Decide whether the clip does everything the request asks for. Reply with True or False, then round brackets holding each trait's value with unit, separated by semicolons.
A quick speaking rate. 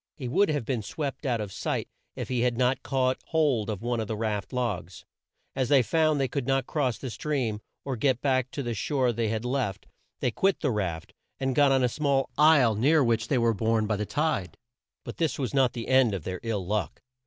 True (230 wpm)